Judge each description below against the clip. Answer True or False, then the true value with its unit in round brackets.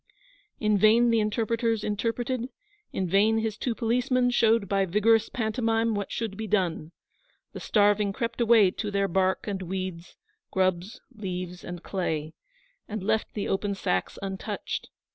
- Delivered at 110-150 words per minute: True (145 wpm)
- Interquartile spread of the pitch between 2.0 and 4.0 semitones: True (3.1 semitones)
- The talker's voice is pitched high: True (210 Hz)